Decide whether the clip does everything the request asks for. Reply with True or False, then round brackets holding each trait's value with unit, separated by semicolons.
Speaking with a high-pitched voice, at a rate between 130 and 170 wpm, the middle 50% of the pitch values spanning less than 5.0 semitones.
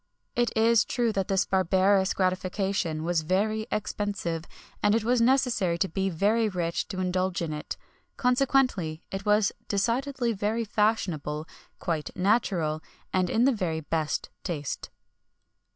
True (195 Hz; 140 wpm; 4.4 semitones)